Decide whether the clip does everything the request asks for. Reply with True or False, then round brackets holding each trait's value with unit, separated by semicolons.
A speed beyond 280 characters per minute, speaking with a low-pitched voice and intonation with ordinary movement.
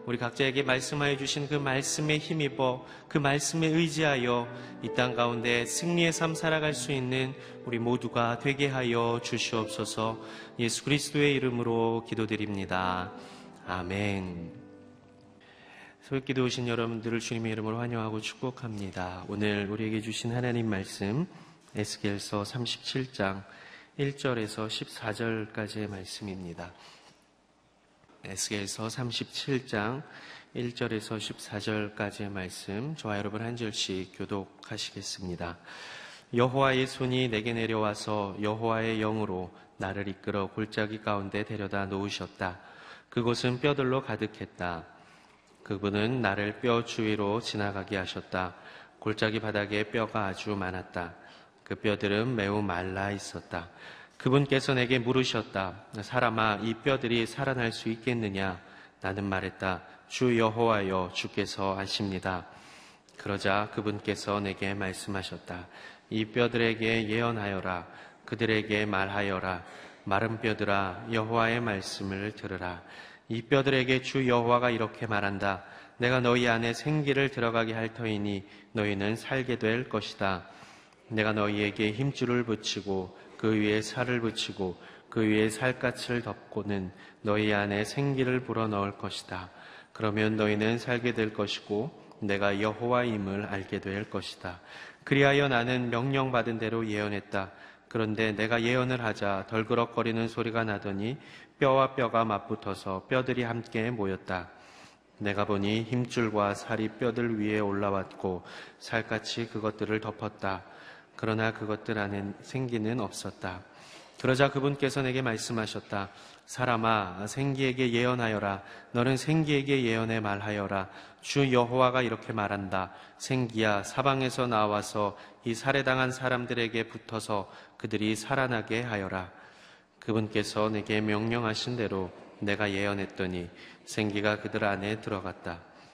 True (290 characters per minute; 110 Hz; 3.2 semitones)